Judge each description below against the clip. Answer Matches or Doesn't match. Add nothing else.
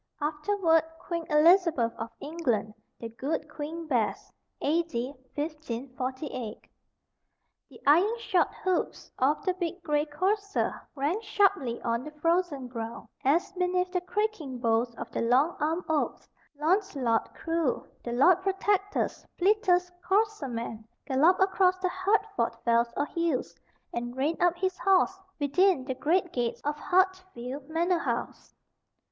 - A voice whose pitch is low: Doesn't match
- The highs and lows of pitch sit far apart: Matches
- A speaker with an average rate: Doesn't match